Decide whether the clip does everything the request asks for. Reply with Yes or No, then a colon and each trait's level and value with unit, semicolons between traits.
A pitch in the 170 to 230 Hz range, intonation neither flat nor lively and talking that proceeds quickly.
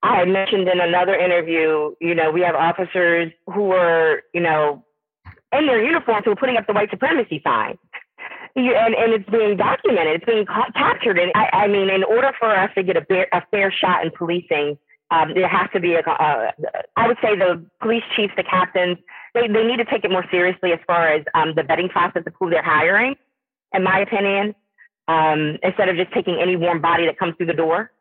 Yes: medium, 185 Hz; average, 3.5 semitones; fast, 215 wpm